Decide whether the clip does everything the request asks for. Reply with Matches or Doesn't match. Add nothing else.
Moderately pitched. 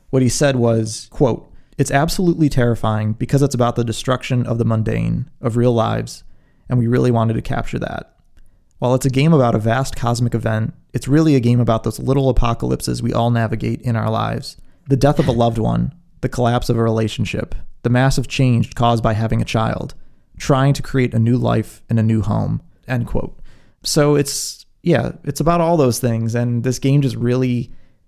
Doesn't match